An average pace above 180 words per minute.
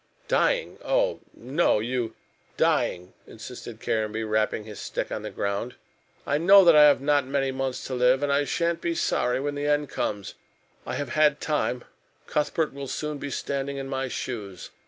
Yes: average, 190 wpm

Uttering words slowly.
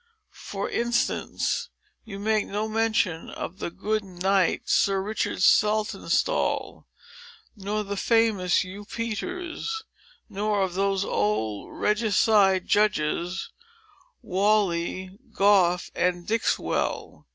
Yes: slow, 100 wpm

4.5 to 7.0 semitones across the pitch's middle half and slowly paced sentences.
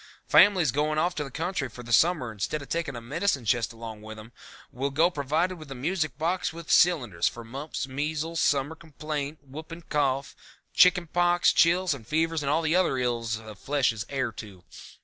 No: average, 5.1 semitones; average, 195 wpm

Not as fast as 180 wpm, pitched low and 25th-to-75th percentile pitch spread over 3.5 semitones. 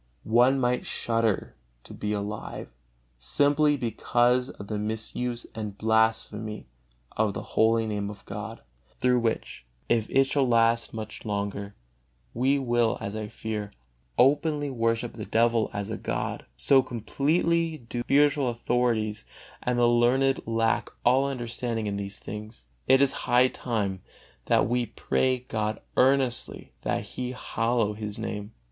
No: average, 140 wpm; low, 115 Hz; average, 2.9 semitones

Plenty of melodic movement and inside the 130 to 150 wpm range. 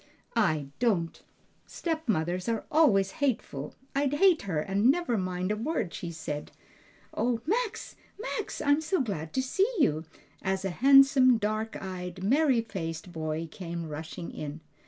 Yes: wide, 8.5 semitones; average, 145 wpm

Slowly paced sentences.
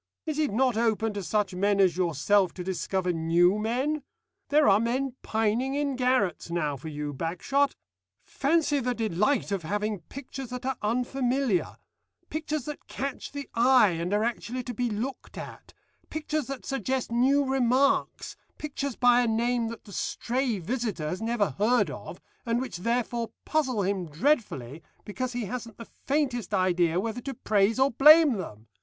No: average, 165 wpm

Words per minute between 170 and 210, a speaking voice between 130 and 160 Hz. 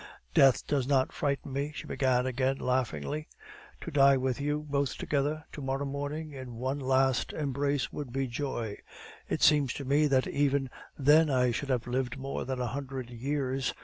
Yes: average, 180 wpm; low, 135 Hz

